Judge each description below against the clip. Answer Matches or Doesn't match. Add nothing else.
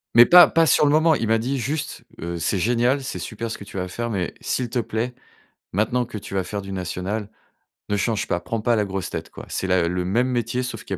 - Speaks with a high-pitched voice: Doesn't match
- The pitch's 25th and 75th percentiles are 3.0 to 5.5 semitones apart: Matches